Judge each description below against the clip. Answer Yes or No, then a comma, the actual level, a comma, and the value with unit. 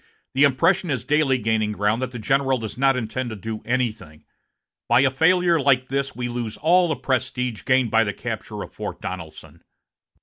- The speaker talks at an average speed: Yes, average, 190 wpm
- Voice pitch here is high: No, low, 125 Hz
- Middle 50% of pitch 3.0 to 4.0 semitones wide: Yes, average, 3.7 semitones